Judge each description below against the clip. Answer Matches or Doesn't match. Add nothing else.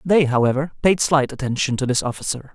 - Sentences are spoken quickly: Doesn't match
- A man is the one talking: Matches